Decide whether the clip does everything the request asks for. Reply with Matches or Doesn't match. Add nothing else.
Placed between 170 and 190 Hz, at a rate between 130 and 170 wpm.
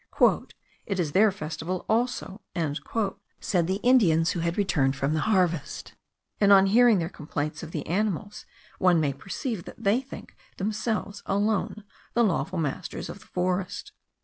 Matches